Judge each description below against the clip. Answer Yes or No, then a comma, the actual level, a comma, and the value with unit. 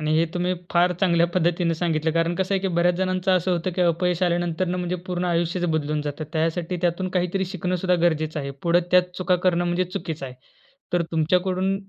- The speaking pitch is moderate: Yes, medium, 175 Hz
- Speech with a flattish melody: Yes, narrow, 1.6 semitones